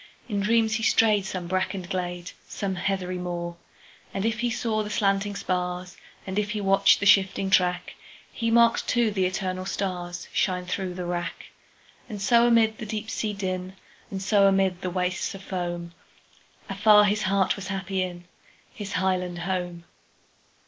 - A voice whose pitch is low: No, high, 190 Hz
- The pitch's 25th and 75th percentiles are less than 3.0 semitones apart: Yes, narrow, 2.4 semitones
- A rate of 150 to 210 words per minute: No, average, 140 wpm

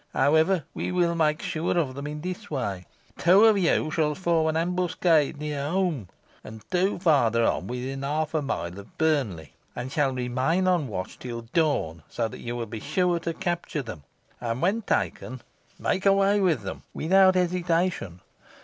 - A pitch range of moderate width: No, wide, 6.3 semitones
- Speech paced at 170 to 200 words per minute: Yes, average, 175 wpm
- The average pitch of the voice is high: No, medium, 155 Hz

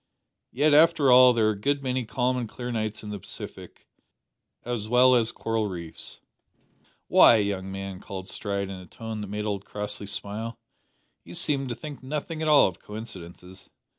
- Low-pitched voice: Yes, low, 110 Hz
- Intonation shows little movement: No, average, 4.2 semitones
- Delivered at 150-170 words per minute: No, average, 180 wpm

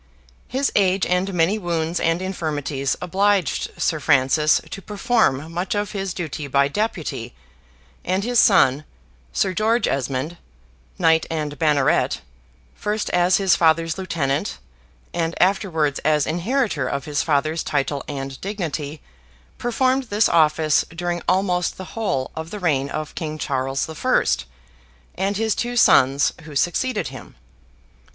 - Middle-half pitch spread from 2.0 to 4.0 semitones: No, average, 5.0 semitones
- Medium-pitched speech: Yes, medium, 165 Hz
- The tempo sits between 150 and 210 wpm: No, slow, 135 wpm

